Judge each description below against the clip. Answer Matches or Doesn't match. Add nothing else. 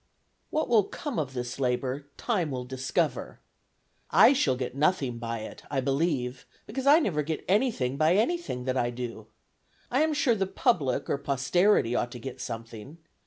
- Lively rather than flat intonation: Matches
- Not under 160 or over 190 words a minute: Matches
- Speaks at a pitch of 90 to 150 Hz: Matches